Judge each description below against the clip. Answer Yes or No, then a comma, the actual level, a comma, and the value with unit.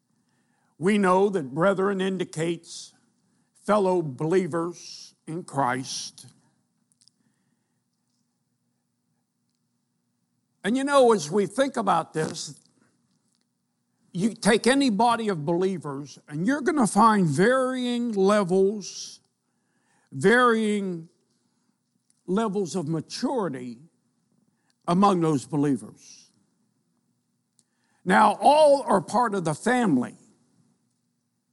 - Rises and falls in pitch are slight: No, average, 5.0 semitones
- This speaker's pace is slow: Yes, slow, 85 wpm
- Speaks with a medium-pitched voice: No, high, 195 Hz